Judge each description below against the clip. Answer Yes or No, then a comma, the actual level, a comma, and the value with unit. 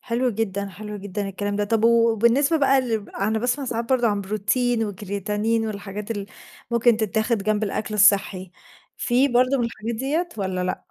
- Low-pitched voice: No, high, 220 Hz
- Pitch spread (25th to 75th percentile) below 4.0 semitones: Yes, average, 2.9 semitones